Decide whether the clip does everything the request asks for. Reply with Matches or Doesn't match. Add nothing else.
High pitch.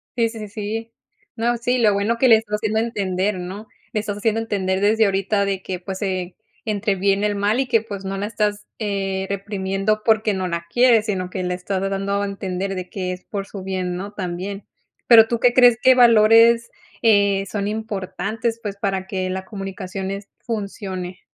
Matches